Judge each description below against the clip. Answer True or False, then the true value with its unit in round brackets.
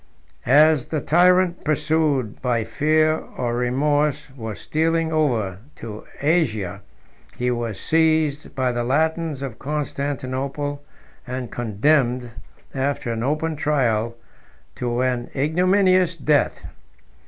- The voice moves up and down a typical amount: True (4.3 semitones)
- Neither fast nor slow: False (110 wpm)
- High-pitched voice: False (140 Hz)